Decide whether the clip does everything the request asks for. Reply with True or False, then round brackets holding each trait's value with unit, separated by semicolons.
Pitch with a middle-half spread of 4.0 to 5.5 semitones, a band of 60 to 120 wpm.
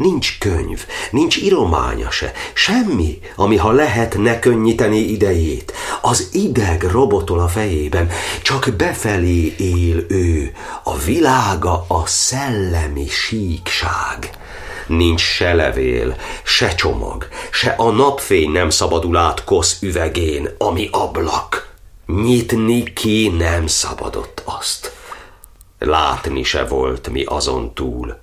True (4.8 semitones; 110 wpm)